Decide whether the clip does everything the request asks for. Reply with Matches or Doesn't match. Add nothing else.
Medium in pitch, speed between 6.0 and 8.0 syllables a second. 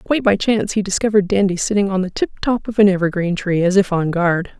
Doesn't match